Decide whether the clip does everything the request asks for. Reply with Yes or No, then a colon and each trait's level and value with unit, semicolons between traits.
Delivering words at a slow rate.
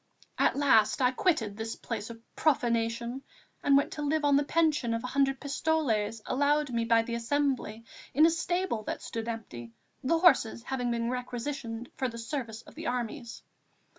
No: average, 175 wpm